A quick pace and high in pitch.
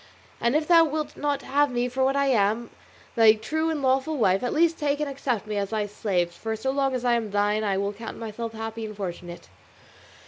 Yes: fast, 230 wpm; high, 235 Hz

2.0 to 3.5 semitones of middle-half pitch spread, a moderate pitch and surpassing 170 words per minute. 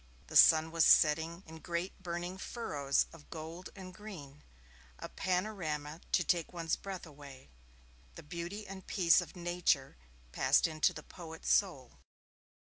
No: average, 2.8 semitones; medium, 170 Hz; average, 140 wpm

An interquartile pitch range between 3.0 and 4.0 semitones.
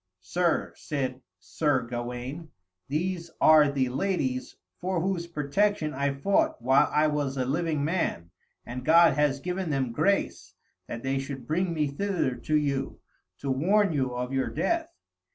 No: average, 4.5 semitones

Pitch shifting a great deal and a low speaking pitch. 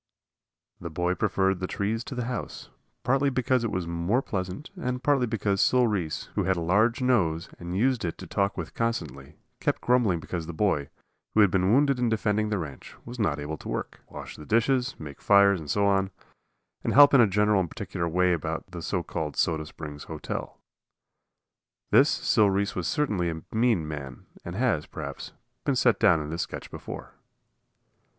Yes: wide, 5.7 semitones; low, 100 Hz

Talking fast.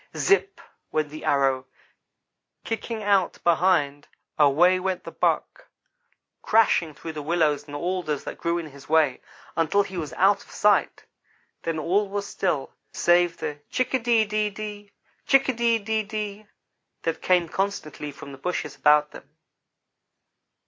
No: average, 150 wpm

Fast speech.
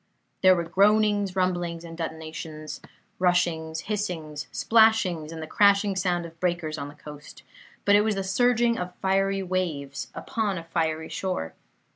No: average, 150 wpm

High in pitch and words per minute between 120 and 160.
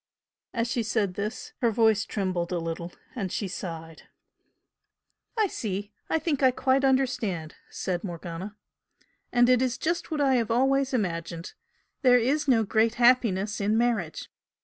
Yes: high, 225 Hz; average, 150 wpm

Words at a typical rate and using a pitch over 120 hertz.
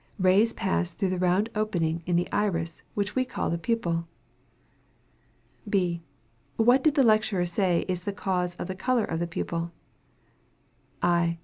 Yes: average, 155 wpm; medium, 185 Hz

